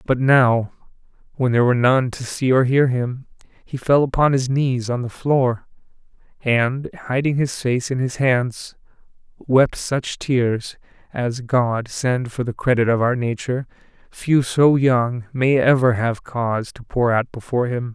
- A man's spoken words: Yes, male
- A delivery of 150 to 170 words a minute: Yes, average, 165 wpm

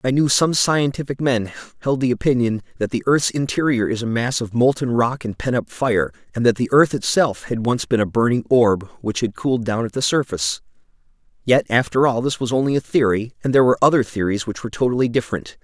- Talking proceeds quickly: Yes, fast, 220 wpm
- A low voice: Yes, low, 120 Hz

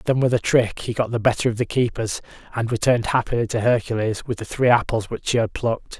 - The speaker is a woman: No, male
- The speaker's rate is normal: No, fast, 240 wpm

